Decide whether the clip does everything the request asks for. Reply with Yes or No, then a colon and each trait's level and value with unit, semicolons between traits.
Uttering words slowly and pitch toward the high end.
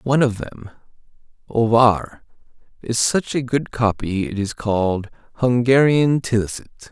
No: slow, 120 wpm; low, 115 Hz